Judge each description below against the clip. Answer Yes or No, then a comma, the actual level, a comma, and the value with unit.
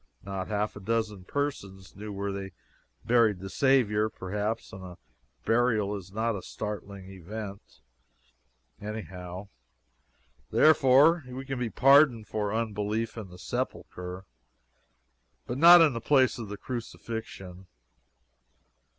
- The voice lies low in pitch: Yes, low, 105 Hz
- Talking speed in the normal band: No, slow, 125 wpm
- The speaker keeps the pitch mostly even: No, average, 3.7 semitones